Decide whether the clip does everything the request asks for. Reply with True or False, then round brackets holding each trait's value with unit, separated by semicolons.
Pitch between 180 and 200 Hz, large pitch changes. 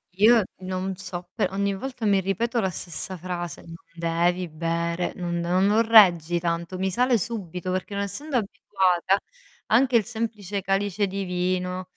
False (190 Hz; 2.9 semitones)